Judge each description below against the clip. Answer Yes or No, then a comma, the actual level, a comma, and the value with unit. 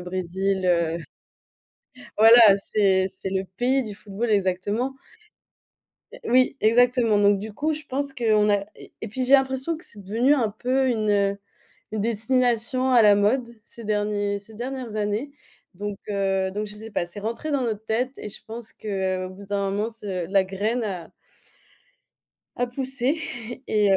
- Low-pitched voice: No, high, 215 Hz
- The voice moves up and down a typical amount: Yes, average, 3.6 semitones